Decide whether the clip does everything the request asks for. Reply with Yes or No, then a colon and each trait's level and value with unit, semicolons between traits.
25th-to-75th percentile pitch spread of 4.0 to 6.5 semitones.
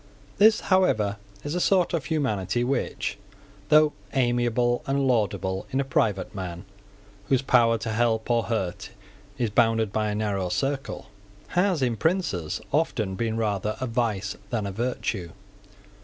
Yes: average, 4.6 semitones